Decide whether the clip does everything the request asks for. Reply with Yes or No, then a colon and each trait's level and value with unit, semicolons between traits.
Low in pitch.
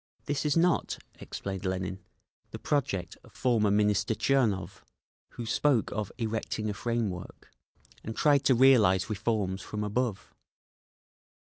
Yes: low, 110 Hz